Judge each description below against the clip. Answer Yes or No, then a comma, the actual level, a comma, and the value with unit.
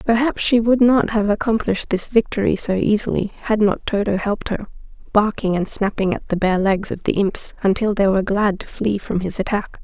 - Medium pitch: No, high, 205 Hz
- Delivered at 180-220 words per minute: Yes, fast, 205 wpm